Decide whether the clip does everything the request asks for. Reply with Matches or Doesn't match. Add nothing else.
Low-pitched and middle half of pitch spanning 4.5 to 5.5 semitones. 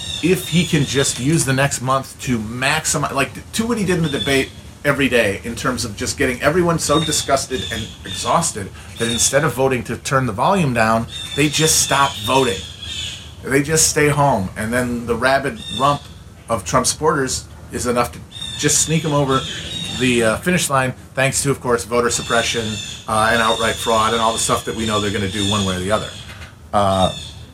Matches